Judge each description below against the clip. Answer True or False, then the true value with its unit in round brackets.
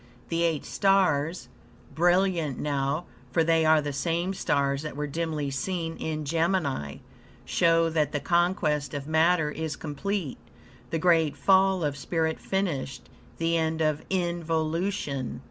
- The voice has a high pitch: False (160 Hz)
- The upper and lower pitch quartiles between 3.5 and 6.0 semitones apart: False (2.8 semitones)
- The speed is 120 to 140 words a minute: True (135 wpm)